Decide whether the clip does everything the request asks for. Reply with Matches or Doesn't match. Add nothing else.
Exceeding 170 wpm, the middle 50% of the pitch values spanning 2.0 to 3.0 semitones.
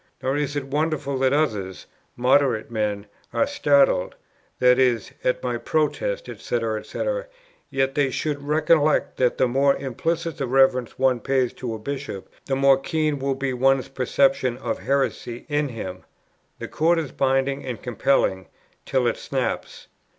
Doesn't match